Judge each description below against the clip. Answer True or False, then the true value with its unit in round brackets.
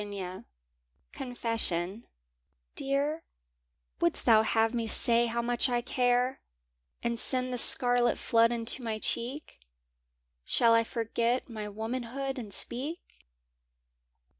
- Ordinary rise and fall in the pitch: False (1.9 semitones)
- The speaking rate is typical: False (110 wpm)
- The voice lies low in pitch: False (235 Hz)